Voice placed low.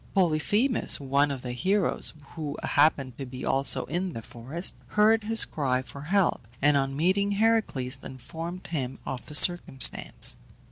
No: medium, 150 Hz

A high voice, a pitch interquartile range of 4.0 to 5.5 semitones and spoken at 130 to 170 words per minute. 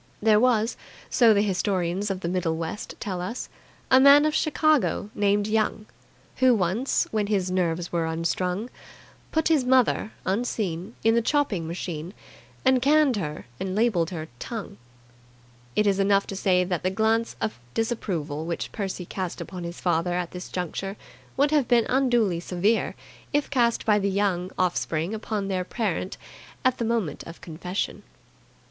Yes: high, 200 Hz; average, 4.5 semitones; average, 160 wpm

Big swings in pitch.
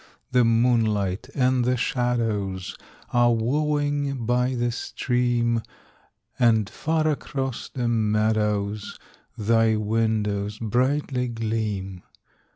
No: average, 2.7 semitones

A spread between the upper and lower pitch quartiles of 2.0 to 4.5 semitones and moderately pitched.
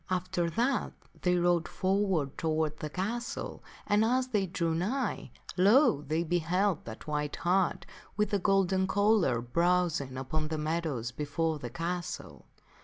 Yes: average, 3.9 semitones; medium, 175 Hz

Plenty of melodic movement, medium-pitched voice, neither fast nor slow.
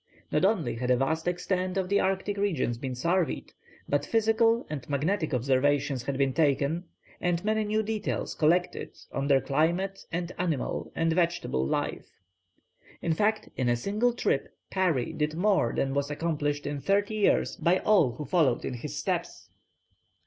Yes: wide, 5.7 semitones; medium, 165 Hz; average, 165 wpm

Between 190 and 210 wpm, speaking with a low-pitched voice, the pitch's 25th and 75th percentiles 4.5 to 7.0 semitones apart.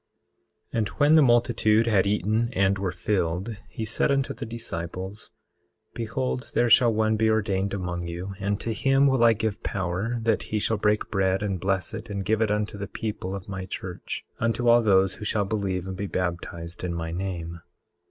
No: average, 195 wpm; low, 105 Hz; average, 3.2 semitones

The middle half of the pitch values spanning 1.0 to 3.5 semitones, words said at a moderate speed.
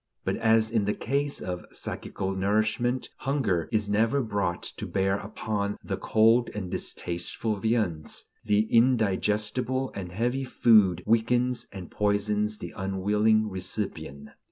No: average, 2.9 semitones; slow, 130 wpm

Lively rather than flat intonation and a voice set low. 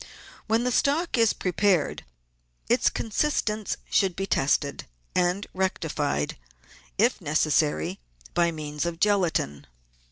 No: wide, 5.8 semitones; medium, 180 Hz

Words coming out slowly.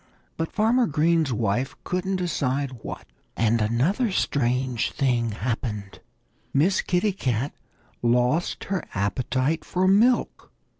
Yes: slow, 110 wpm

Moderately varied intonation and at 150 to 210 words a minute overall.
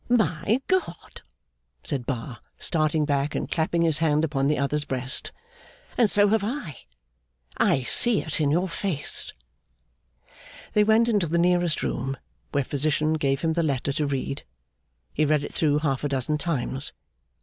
Yes: average, 3.8 semitones; average, 160 wpm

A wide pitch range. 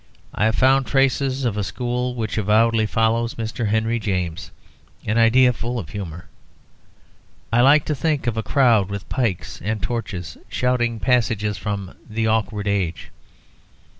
No: average, 3.2 semitones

